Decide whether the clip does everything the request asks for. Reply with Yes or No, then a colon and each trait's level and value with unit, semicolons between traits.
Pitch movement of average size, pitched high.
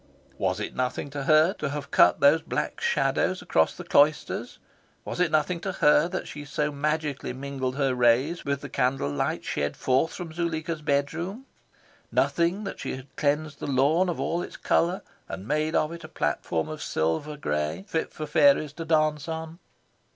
No: average, 3.2 semitones; medium, 150 Hz